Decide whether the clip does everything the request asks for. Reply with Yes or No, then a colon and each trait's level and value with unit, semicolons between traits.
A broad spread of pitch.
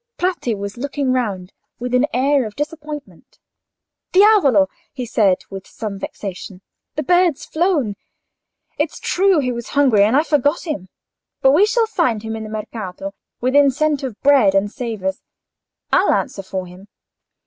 Yes: wide, 6.3 semitones